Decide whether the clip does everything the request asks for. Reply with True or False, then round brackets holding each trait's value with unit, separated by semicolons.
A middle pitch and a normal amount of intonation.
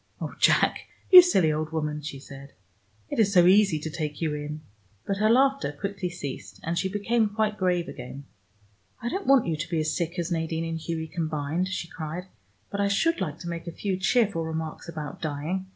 True (170 Hz; 4.2 semitones)